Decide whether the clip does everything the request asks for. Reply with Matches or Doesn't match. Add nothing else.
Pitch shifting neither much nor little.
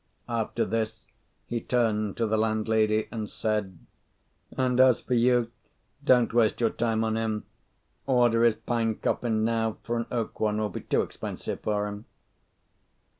Doesn't match